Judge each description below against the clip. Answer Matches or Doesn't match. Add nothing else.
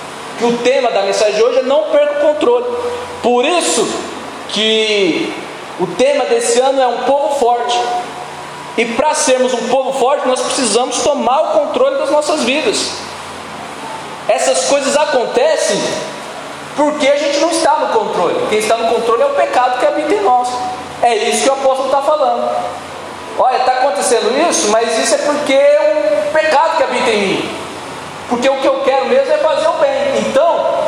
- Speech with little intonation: Doesn't match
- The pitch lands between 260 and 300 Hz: Matches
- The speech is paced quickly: Doesn't match